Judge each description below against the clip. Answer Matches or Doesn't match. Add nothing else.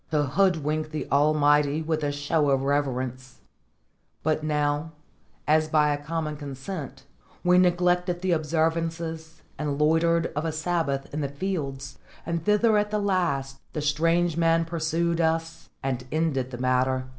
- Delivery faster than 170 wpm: Doesn't match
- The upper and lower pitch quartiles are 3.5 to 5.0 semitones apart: Doesn't match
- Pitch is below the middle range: Doesn't match